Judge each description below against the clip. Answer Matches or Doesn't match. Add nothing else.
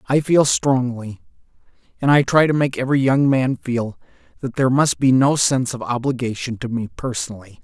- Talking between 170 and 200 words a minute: Matches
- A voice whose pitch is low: Matches